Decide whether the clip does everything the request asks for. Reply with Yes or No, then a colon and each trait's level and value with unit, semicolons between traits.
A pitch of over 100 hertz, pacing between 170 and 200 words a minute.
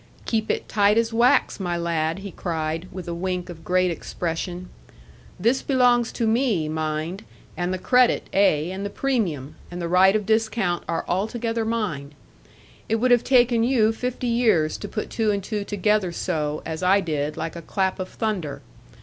Yes: high, 190 Hz; average, 180 wpm